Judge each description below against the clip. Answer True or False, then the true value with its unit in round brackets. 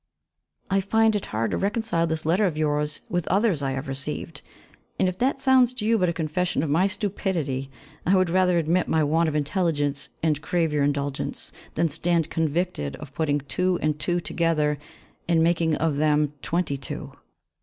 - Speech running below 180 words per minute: False (185 wpm)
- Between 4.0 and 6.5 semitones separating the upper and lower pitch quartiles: False (3.6 semitones)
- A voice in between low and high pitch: True (165 Hz)